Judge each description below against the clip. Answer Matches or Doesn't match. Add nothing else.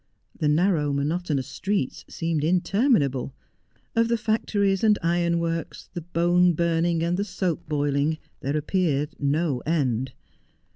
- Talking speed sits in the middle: Doesn't match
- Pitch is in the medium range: Matches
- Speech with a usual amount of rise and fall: Matches